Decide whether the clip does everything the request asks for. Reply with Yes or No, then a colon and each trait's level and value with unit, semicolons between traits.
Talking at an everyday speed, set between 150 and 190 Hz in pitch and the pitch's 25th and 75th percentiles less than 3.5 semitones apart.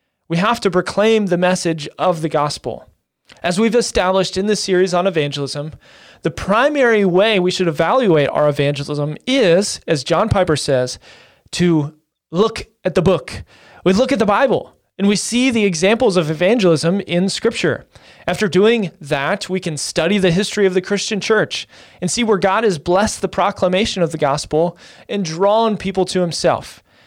No: average, 170 wpm; medium, 185 Hz; average, 3.9 semitones